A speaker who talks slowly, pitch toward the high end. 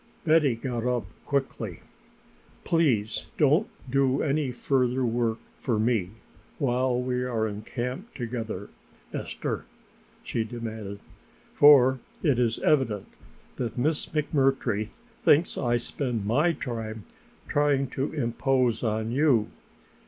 No: slow, 115 wpm; low, 125 Hz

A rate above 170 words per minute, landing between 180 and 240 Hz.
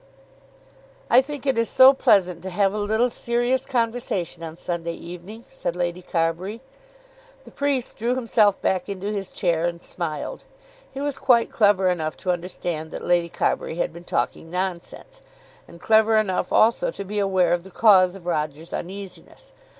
No: average, 165 wpm; high, 190 Hz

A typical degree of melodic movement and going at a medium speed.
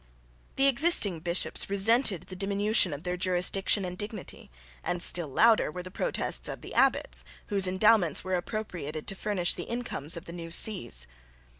Yes: average, 3.5 semitones; average, 165 wpm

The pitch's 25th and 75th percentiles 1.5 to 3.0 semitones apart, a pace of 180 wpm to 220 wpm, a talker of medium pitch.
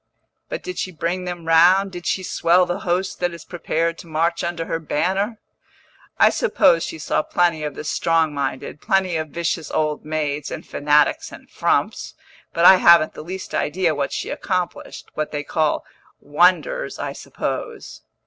No: average, 2.7 semitones; average, 170 wpm; medium, 170 Hz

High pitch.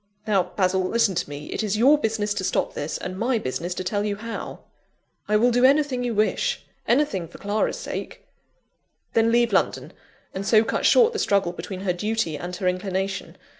Yes: high, 205 Hz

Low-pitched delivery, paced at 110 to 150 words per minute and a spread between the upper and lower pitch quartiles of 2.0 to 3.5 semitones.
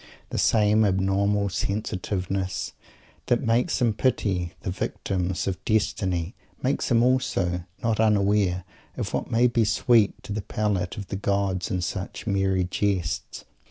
Yes: low, 100 Hz; average, 140 wpm; average, 2.7 semitones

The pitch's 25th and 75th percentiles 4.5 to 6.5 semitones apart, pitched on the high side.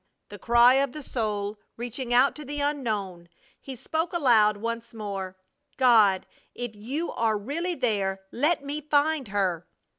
Yes: wide, 5.5 semitones; high, 240 Hz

